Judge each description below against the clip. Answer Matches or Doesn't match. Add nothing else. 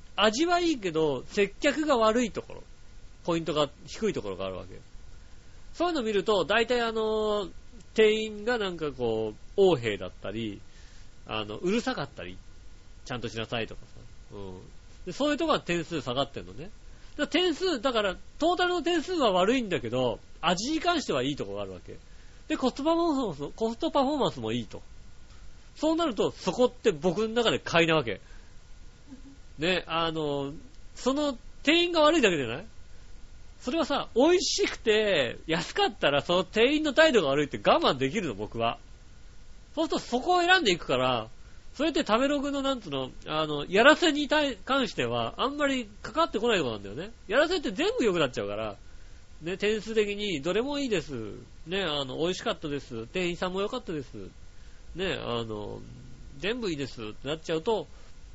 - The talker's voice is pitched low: Doesn't match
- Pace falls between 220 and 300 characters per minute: Doesn't match